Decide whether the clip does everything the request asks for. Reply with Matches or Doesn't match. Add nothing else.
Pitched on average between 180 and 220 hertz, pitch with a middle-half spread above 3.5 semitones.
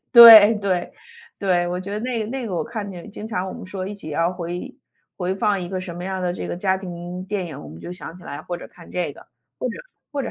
Doesn't match